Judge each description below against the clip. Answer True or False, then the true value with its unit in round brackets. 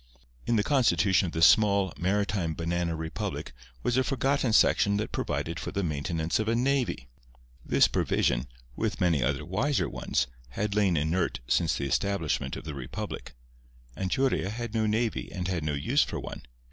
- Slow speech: False (160 wpm)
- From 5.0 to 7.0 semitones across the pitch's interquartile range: True (5.5 semitones)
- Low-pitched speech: True (90 Hz)